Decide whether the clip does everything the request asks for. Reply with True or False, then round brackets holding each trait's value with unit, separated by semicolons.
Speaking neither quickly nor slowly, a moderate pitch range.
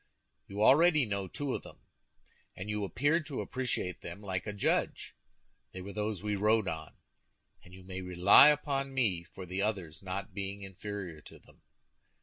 True (170 wpm; 3.5 semitones)